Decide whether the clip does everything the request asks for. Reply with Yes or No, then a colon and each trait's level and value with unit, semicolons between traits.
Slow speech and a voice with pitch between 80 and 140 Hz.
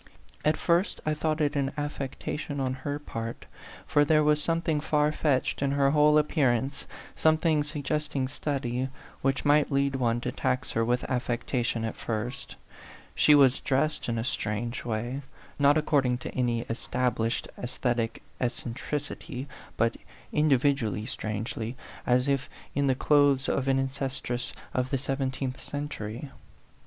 No: average, 145 wpm; low, 135 Hz